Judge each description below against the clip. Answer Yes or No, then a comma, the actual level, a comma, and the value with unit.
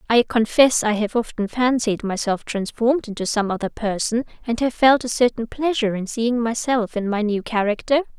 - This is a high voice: Yes, high, 230 Hz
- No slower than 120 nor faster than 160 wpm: No, average, 185 wpm